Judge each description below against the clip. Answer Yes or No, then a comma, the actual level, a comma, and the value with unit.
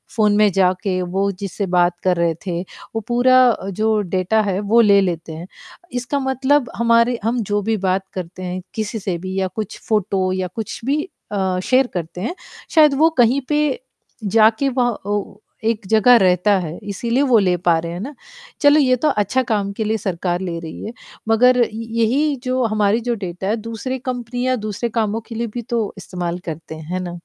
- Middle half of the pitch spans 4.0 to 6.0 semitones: Yes, average, 4.5 semitones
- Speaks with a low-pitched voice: No, high, 215 Hz